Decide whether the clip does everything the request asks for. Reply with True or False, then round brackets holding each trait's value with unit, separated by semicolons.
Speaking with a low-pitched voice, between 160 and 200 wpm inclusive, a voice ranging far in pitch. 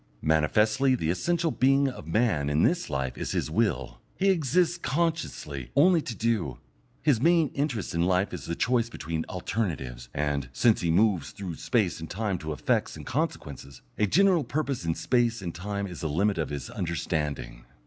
True (100 Hz; 180 wpm; 8.9 semitones)